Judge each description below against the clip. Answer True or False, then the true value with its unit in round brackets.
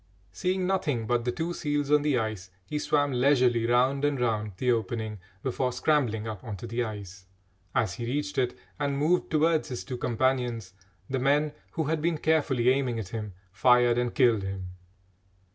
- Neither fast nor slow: True (180 wpm)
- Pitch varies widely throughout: False (4.4 semitones)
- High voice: False (125 Hz)